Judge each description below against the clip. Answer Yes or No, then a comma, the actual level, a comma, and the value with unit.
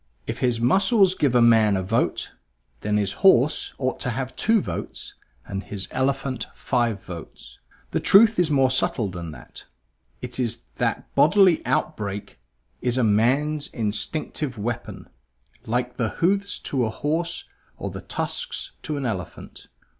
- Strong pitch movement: Yes, wide, 5.9 semitones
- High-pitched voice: No, low, 125 Hz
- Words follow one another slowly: No, average, 150 wpm